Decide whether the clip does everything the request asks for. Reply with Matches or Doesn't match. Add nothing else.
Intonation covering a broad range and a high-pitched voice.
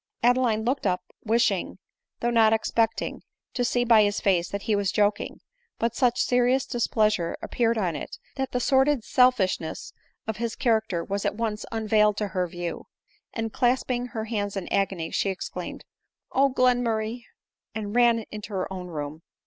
Doesn't match